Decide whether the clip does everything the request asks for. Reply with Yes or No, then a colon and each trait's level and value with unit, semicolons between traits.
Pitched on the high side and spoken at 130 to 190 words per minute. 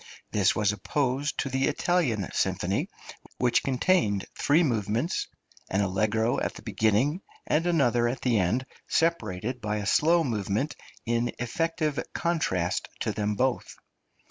No: low, 120 Hz; slow, 135 wpm